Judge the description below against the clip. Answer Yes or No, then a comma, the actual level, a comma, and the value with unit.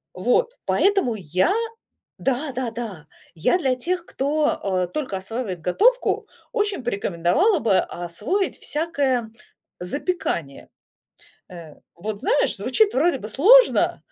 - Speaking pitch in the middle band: No, very high, 255 Hz